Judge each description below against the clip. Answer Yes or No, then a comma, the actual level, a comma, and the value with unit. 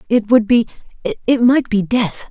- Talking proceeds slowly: Yes, slow, 130 wpm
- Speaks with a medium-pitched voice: No, high, 230 Hz